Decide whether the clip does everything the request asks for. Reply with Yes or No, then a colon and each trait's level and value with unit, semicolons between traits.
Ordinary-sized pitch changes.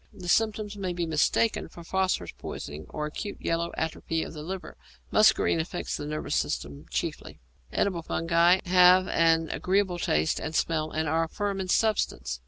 Yes: average, 3.1 semitones